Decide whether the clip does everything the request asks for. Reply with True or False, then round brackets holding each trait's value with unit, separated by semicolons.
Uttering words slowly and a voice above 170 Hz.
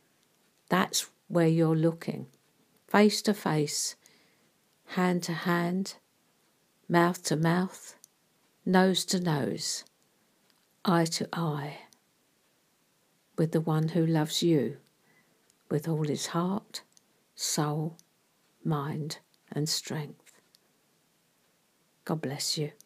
False (95 wpm; 165 Hz)